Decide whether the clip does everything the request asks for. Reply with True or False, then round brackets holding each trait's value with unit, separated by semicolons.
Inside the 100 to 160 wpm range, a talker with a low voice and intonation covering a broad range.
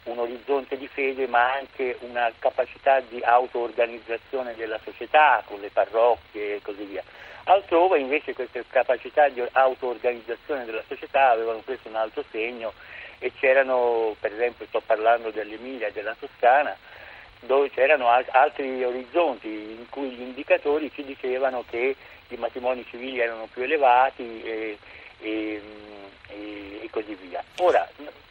False (140 wpm; 125 Hz; 2.9 semitones)